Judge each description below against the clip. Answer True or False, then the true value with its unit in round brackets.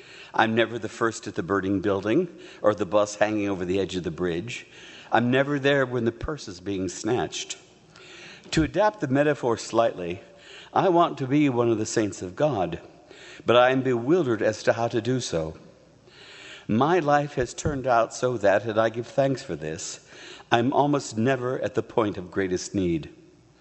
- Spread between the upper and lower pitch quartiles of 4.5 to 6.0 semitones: True (4.8 semitones)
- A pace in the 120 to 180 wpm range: False (190 wpm)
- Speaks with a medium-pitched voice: False (115 Hz)